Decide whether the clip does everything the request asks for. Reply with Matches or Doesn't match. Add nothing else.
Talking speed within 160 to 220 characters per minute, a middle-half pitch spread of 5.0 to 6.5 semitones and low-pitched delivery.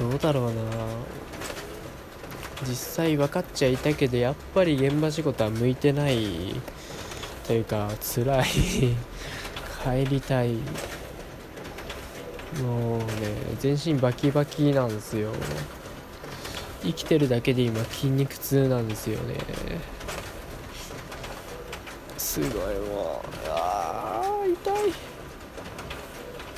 Doesn't match